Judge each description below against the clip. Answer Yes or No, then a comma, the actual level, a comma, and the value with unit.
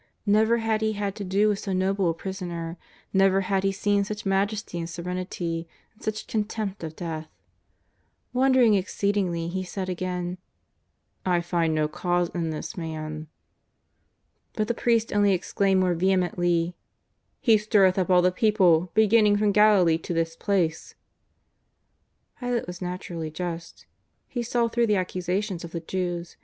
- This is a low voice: No, medium, 185 Hz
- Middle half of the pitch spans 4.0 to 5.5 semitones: No, average, 3.2 semitones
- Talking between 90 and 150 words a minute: No, average, 160 wpm